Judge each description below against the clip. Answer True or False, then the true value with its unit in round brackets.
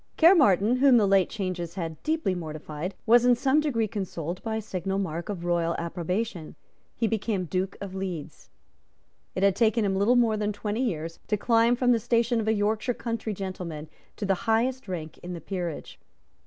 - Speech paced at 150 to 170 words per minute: False (185 wpm)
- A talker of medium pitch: False (200 Hz)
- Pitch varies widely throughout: False (4.4 semitones)